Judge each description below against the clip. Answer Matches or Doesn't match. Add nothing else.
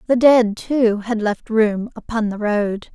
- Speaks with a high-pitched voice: Matches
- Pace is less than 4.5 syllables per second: Matches